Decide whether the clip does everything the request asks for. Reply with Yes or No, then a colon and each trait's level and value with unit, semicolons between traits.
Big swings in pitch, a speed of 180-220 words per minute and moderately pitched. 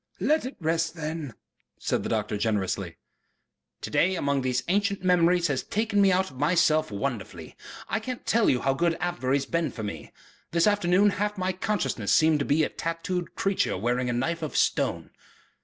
Yes: wide, 6.1 semitones; average, 190 wpm; medium, 165 Hz